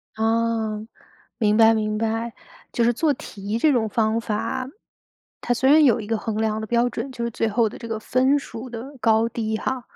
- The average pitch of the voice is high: Yes, high, 230 Hz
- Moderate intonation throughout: No, narrow, 1.8 semitones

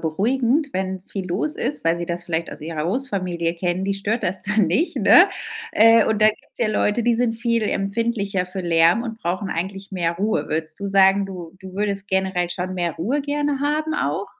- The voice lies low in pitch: No, high, 195 Hz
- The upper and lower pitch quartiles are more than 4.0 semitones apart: Yes, average, 4.5 semitones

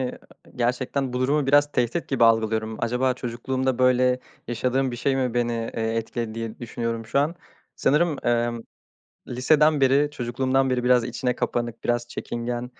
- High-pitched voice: No, low, 125 Hz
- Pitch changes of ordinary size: No, narrow, 2.1 semitones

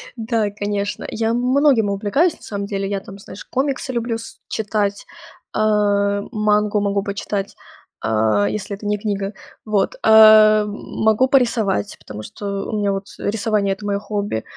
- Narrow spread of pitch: Yes, narrow, 1.6 semitones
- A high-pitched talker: Yes, high, 205 Hz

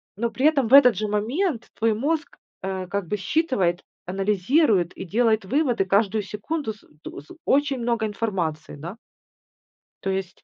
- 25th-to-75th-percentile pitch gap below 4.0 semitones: No, average, 5.3 semitones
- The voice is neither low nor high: No, high, 215 Hz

